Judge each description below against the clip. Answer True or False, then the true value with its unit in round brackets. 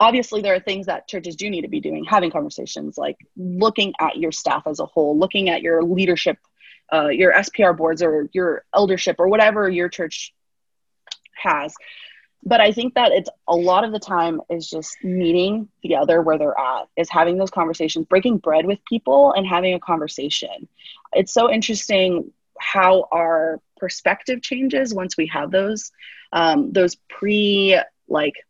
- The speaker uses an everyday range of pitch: True (3.6 semitones)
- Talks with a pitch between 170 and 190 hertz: True (185 Hz)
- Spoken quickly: False (170 wpm)